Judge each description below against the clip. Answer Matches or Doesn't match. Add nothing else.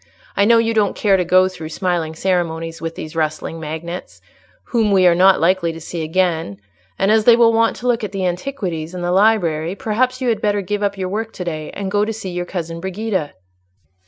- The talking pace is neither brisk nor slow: Doesn't match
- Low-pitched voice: Doesn't match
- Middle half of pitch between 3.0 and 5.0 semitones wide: Matches